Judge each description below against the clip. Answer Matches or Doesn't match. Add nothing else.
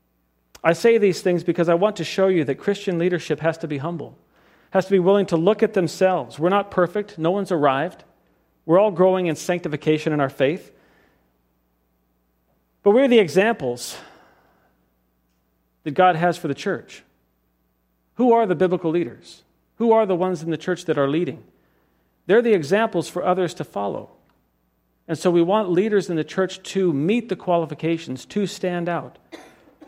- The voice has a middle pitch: Matches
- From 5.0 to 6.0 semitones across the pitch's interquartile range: Matches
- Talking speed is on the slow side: Doesn't match